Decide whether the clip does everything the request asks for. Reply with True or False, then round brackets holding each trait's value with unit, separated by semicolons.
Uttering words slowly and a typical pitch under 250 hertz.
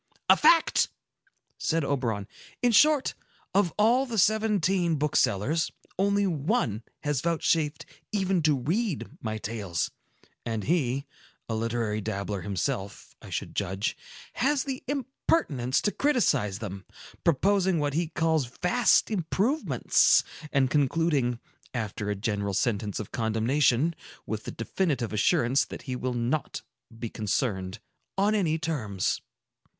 True (120 wpm; 140 Hz)